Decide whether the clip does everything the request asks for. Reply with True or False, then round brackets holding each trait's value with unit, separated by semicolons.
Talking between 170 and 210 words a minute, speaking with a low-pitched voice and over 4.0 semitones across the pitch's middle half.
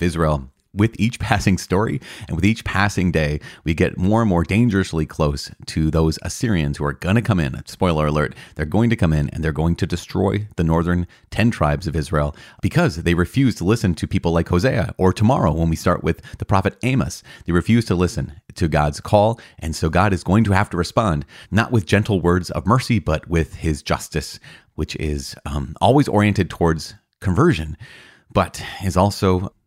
True (200 wpm; 90 Hz; 4.9 semitones)